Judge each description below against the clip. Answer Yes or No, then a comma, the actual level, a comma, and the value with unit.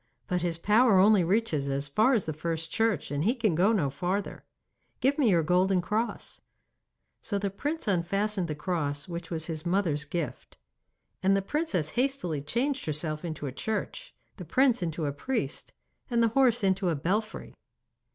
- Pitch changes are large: Yes, wide, 5.7 semitones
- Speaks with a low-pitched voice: No, medium, 185 Hz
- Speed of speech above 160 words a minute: Yes, average, 175 wpm